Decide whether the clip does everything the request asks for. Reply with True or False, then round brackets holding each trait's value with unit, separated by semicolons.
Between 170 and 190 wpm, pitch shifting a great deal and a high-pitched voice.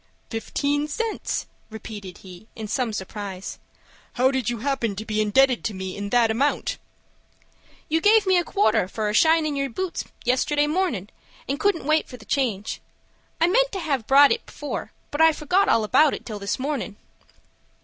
True (180 wpm; 6.2 semitones; 260 Hz)